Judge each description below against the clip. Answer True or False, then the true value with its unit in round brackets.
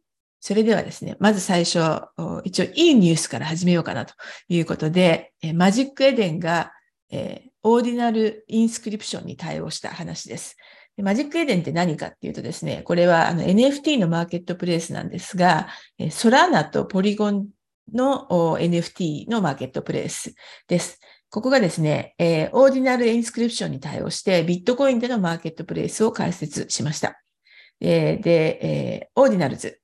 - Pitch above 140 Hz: True (190 Hz)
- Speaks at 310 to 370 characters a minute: False (380 characters per minute)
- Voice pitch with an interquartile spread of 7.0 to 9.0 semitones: False (5.7 semitones)